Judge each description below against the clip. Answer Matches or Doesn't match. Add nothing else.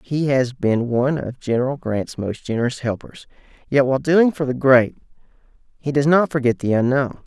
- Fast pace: Doesn't match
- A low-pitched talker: Matches